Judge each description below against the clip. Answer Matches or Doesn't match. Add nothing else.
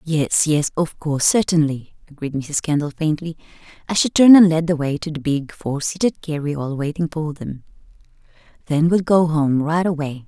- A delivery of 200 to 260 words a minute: Doesn't match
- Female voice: Matches